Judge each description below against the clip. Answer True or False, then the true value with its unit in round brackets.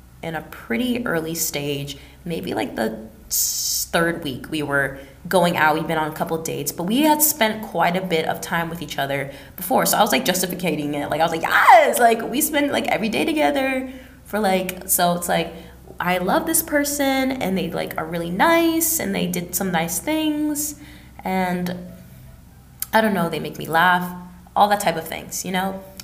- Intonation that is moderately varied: False (5.9 semitones)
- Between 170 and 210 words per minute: True (200 wpm)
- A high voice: False (180 Hz)